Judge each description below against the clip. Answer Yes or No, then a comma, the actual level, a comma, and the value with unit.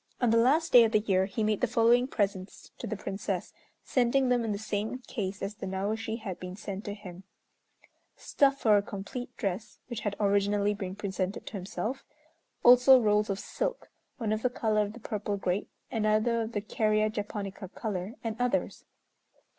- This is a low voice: No, high, 215 Hz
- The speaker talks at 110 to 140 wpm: No, average, 185 wpm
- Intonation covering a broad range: No, narrow, 2.6 semitones